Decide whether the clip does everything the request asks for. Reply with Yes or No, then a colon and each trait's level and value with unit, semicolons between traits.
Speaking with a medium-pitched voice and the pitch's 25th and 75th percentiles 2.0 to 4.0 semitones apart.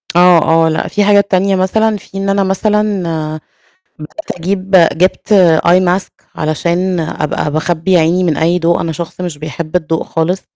Yes: medium, 180 Hz; average, 3.0 semitones